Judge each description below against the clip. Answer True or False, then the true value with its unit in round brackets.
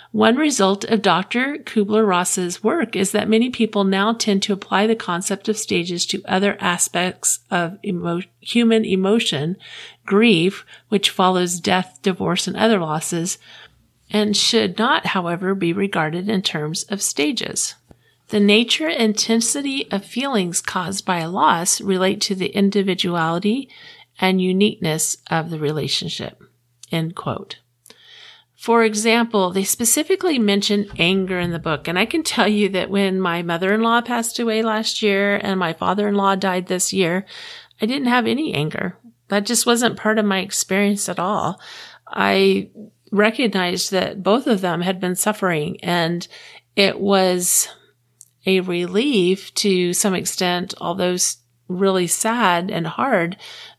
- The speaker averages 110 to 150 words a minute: True (145 wpm)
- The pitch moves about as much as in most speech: True (3.3 semitones)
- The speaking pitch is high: True (195 Hz)